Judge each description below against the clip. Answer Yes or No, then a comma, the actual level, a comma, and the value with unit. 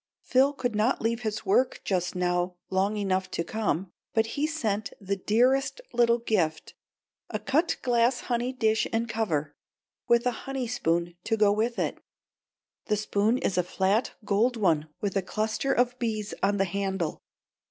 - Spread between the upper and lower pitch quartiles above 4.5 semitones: No, average, 3.9 semitones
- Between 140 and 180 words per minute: Yes, average, 165 wpm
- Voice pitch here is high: Yes, high, 215 Hz